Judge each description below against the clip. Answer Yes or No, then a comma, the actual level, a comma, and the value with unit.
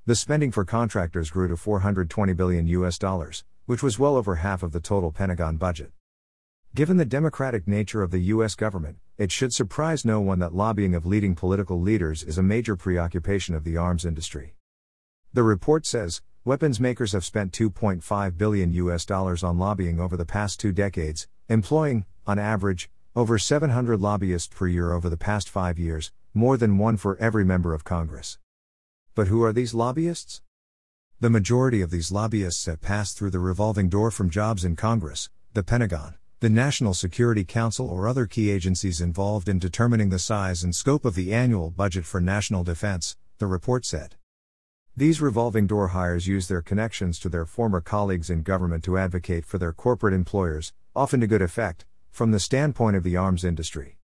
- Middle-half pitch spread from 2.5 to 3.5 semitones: No, average, 4.2 semitones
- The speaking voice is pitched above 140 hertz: No, very low, 95 Hz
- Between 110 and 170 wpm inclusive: No, average, 180 wpm